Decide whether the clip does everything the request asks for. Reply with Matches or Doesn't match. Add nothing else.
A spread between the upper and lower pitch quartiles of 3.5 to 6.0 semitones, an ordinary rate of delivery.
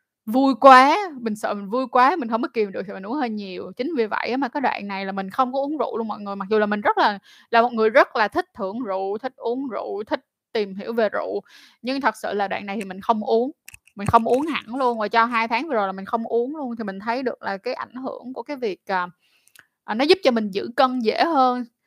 Doesn't match